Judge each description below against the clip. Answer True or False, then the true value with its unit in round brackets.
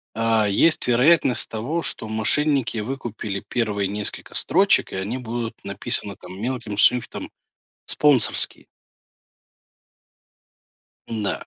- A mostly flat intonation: False (3.3 semitones)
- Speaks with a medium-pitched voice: False (115 Hz)